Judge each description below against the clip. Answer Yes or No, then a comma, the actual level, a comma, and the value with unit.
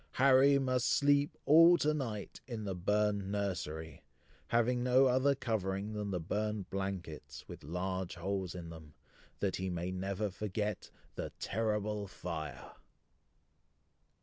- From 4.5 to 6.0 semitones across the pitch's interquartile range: Yes, average, 4.8 semitones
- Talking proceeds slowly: Yes, slow, 130 wpm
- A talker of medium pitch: No, low, 100 Hz